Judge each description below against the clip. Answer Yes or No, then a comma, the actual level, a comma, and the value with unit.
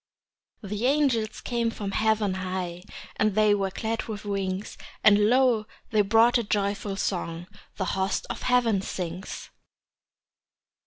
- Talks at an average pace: No, slow, 130 wpm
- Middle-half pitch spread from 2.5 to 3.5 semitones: Yes, average, 2.8 semitones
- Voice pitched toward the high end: Yes, high, 210 Hz